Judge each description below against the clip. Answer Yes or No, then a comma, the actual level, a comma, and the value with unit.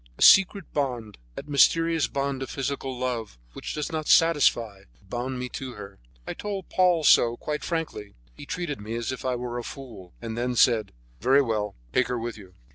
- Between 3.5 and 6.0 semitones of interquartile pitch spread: Yes, average, 4.3 semitones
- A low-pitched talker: Yes, low, 125 Hz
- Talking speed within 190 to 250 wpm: Yes, average, 195 wpm